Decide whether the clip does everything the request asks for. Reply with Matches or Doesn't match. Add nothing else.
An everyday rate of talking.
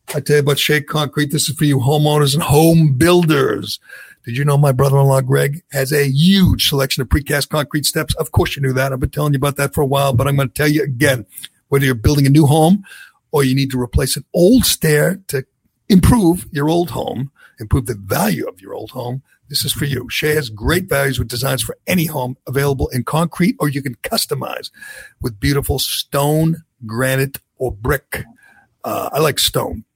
Doesn't match